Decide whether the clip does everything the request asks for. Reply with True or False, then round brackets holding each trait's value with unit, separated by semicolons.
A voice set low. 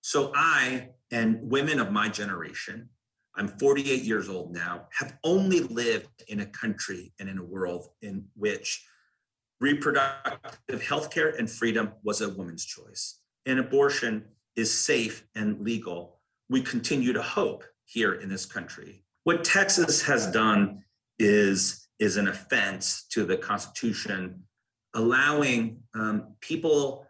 True (115 Hz)